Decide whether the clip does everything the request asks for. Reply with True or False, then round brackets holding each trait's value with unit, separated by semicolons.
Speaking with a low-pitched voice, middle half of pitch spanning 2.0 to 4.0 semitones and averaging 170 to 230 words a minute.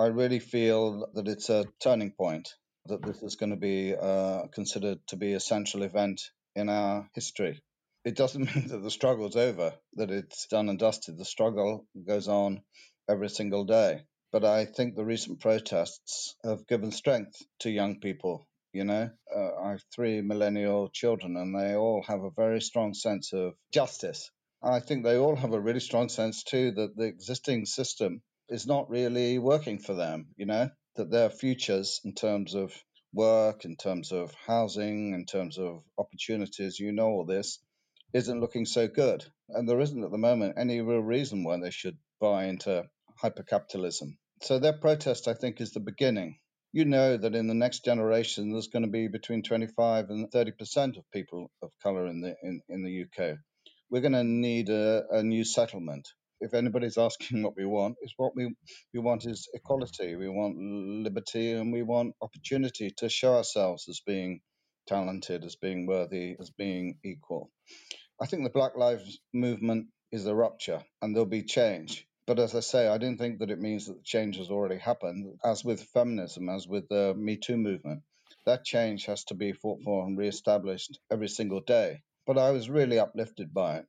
True (110 Hz; 3.1 semitones; 190 wpm)